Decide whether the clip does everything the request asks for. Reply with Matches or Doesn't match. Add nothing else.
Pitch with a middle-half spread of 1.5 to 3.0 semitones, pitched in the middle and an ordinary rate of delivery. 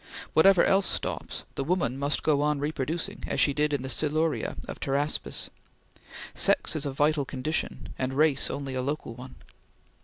Matches